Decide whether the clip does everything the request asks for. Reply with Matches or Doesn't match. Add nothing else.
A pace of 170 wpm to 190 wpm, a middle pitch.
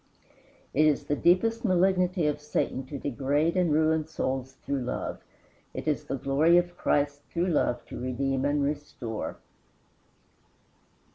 Doesn't match